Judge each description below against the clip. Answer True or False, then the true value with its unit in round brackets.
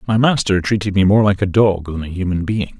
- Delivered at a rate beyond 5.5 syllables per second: True (5.7 syllables/s)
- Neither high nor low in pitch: False (100 Hz)